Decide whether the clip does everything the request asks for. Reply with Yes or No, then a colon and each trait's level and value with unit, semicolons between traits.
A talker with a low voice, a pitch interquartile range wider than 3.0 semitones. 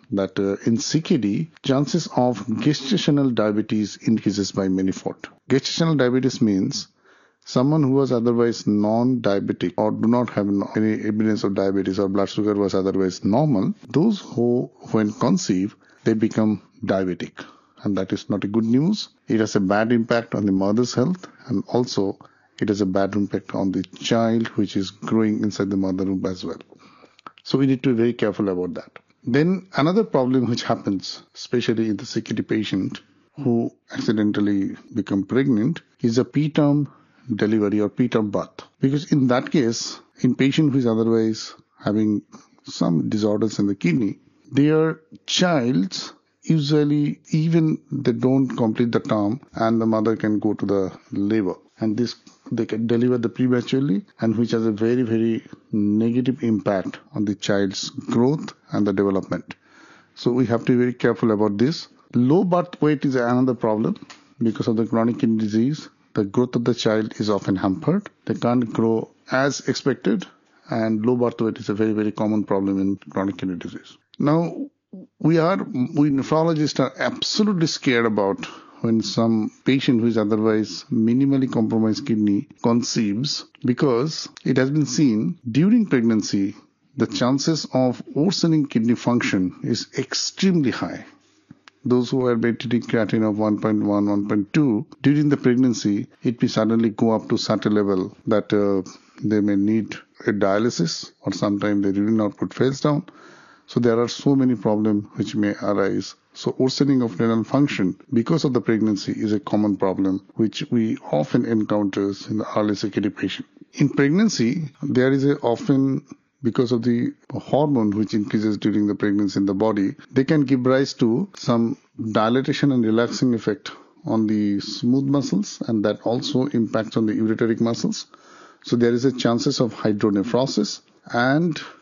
Yes: low, 115 Hz; average, 3.8 semitones